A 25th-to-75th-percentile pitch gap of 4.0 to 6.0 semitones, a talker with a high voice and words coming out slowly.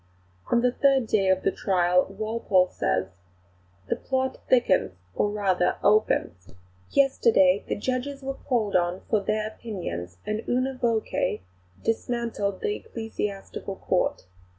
Yes: average, 4.5 semitones; high, 215 Hz; slow, 130 wpm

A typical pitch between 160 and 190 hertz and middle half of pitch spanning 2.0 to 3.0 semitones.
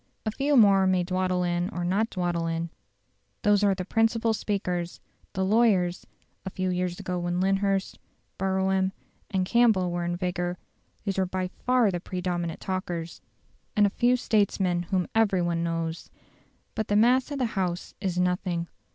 Yes: medium, 185 Hz; narrow, 2.6 semitones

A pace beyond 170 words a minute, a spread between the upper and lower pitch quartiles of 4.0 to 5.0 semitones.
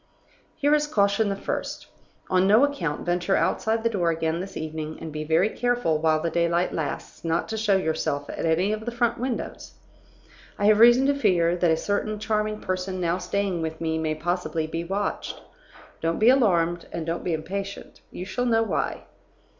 Yes: average, 190 wpm; average, 4.6 semitones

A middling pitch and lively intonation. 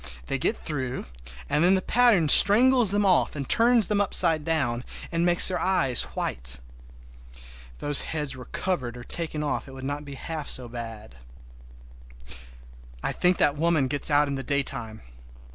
Yes: medium, 150 Hz; wide, 5.9 semitones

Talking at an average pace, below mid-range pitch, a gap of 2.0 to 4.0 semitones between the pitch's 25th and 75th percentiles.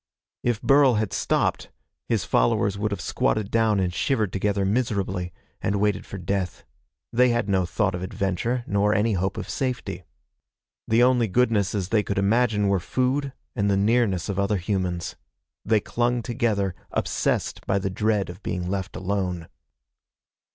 Yes: average, 160 wpm; low, 100 Hz; average, 3.1 semitones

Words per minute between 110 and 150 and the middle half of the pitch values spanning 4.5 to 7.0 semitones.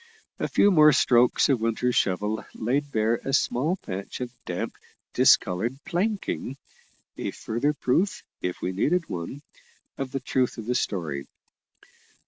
Yes: average, 140 wpm; average, 4.9 semitones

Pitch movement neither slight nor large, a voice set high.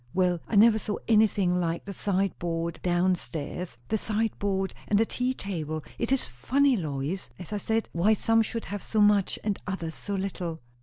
Yes: average, 4.0 semitones; high, 195 Hz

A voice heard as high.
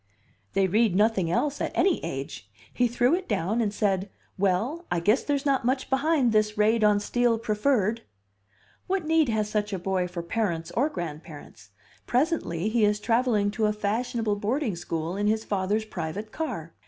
Yes: high, 215 Hz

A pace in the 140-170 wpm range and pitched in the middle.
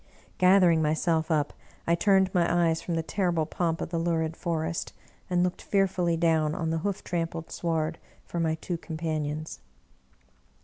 Yes: average, 160 wpm; medium, 165 Hz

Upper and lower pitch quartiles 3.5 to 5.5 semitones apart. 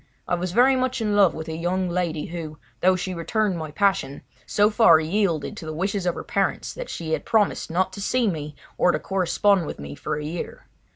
Yes: average, 4.2 semitones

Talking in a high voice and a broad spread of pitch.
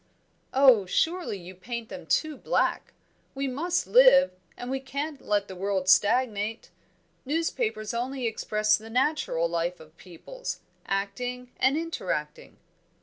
Yes: high, 245 Hz; wide, 5.9 semitones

